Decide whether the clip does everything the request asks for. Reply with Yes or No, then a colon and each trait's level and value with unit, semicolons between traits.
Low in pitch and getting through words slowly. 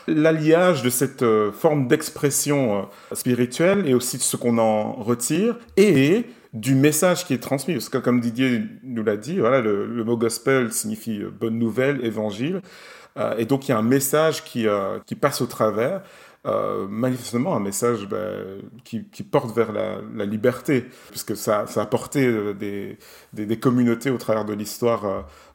No: low, 125 Hz; average, 185 wpm